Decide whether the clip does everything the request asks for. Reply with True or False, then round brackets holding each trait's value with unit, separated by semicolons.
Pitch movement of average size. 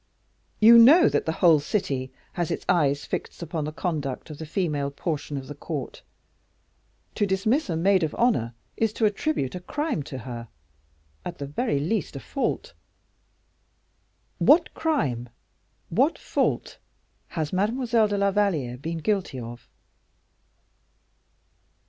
False (6.9 semitones)